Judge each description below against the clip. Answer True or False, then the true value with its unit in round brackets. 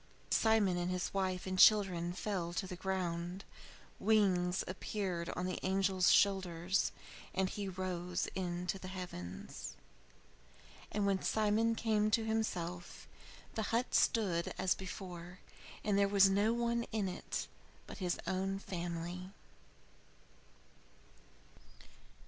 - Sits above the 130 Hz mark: True (190 Hz)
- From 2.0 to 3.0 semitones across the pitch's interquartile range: True (2.4 semitones)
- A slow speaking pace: True (120 wpm)